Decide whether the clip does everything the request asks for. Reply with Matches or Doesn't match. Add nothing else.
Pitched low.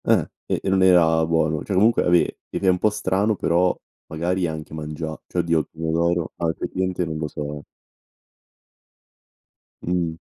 Matches